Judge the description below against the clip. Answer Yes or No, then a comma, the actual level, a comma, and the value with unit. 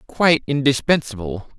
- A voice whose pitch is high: No, low, 135 Hz